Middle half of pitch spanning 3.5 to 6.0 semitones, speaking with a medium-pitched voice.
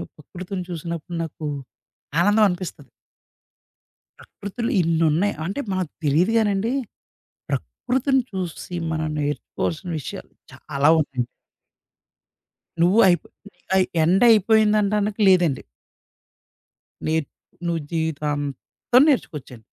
Yes: average, 4.7 semitones; medium, 175 Hz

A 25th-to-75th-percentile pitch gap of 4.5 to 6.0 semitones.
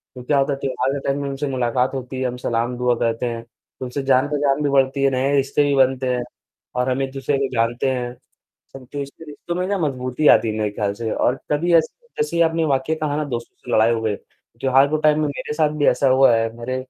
No: average, 2.7 semitones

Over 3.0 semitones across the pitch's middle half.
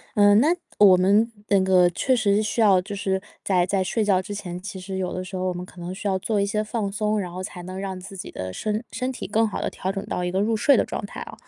No: narrow, 2.4 semitones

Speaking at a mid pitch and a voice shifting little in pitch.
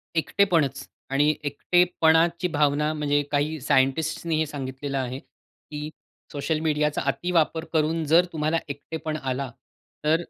Yes: medium, 150 Hz; narrow, 2.2 semitones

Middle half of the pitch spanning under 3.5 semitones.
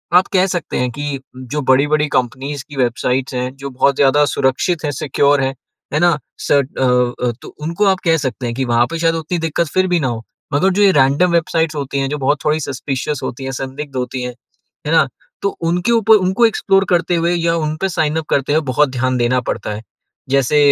No: average, 4.2 semitones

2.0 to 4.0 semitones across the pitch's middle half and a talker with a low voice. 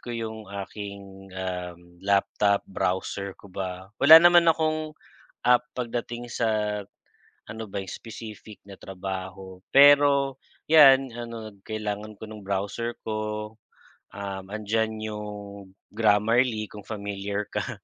Yes: average, 3.0 semitones; low, 105 Hz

